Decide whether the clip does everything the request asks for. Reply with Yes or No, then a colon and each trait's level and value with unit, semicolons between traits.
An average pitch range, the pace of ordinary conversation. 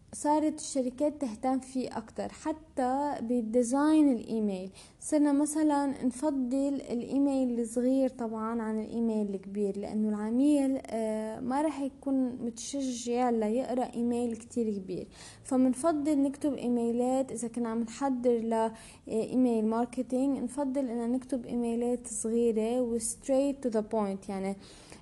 Yes: average, 3.2 semitones; average, 115 wpm